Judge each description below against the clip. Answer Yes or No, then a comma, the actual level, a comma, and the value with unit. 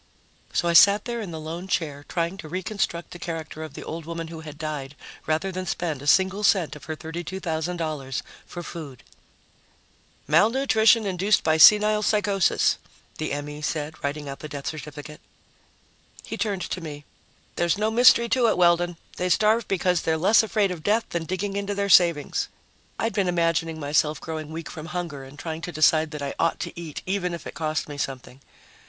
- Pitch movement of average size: Yes, average, 3.8 semitones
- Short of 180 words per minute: No, average, 185 wpm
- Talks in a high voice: No, medium, 170 Hz